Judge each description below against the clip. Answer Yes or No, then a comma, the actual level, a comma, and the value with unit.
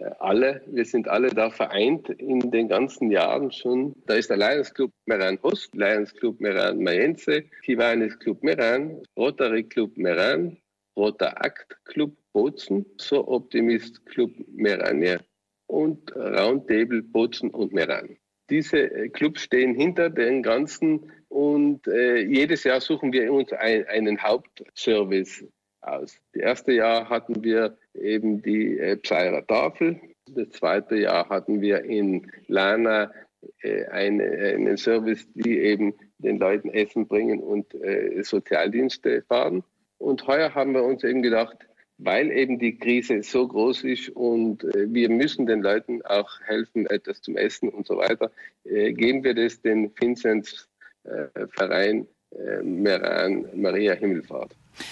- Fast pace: No, average, 140 wpm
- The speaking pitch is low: Yes, low, 120 Hz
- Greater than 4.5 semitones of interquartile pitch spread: Yes, average, 5.1 semitones